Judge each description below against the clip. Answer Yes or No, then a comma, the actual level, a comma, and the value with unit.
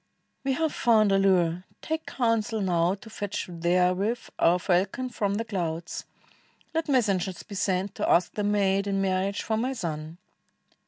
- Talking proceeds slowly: No, average, 160 wpm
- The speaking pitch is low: No, high, 195 Hz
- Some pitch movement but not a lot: Yes, average, 3.5 semitones